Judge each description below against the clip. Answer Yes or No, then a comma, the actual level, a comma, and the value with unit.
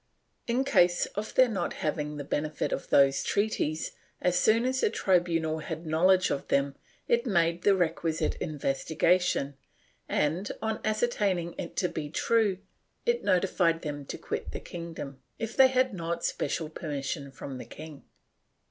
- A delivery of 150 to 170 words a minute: Yes, average, 155 wpm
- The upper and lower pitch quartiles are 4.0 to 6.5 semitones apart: Yes, average, 5.2 semitones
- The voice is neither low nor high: Yes, medium, 170 Hz